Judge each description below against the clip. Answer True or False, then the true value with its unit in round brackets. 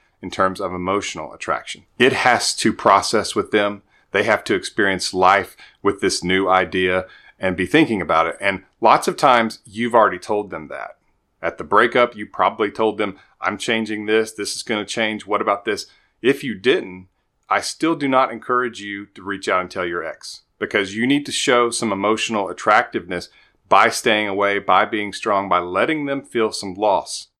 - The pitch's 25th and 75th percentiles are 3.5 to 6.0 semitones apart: False (3.0 semitones)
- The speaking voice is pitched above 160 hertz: False (105 Hz)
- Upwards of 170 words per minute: True (195 wpm)